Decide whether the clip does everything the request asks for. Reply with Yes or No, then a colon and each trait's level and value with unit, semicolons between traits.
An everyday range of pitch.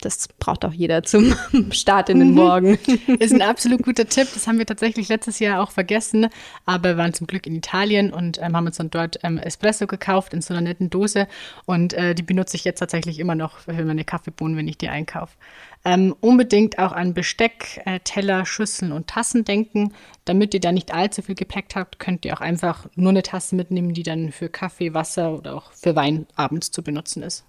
Yes: average, 3.6 semitones